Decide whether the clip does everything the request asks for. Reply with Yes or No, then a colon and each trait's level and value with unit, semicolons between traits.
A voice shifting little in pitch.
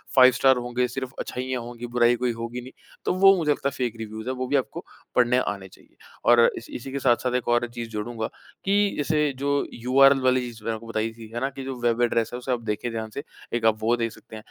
Yes: narrow, 2.2 semitones